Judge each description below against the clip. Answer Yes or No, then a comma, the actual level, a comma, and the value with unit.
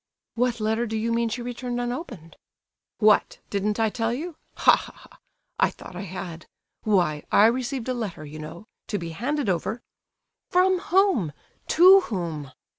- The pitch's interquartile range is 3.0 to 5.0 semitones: No, wide, 5.6 semitones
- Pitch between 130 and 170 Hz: No, high, 225 Hz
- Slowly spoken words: No, average, 165 wpm